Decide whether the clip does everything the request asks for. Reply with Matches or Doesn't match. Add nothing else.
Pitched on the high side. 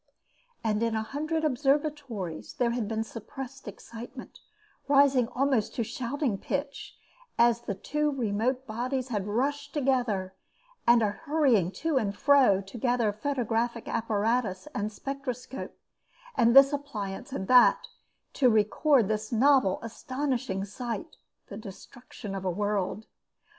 Matches